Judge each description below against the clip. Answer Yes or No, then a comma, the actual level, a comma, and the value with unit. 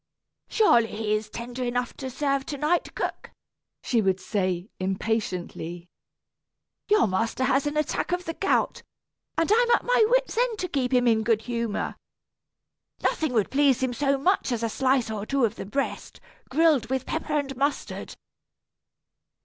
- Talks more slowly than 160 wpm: No, average, 165 wpm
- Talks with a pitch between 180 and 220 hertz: No, very high, 260 Hz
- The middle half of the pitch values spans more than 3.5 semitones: Yes, average, 5.3 semitones